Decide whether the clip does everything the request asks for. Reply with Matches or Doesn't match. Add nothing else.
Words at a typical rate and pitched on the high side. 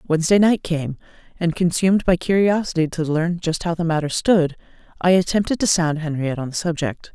Doesn't match